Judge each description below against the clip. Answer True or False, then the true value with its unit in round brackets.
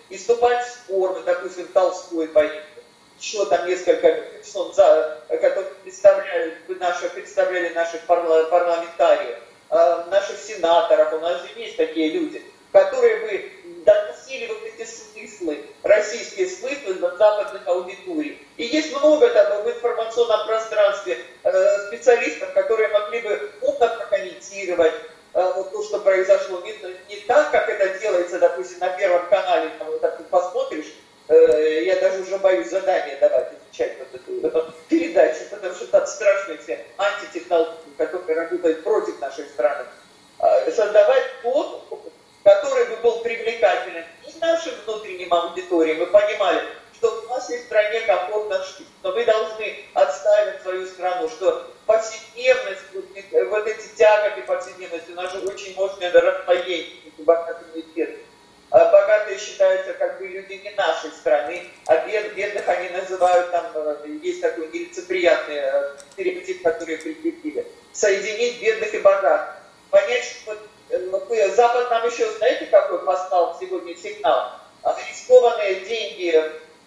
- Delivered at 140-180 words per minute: False (130 wpm)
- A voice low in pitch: False (210 Hz)